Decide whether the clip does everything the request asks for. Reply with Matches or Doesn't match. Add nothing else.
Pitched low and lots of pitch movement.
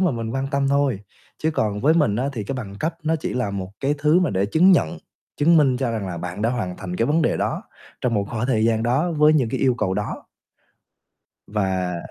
Matches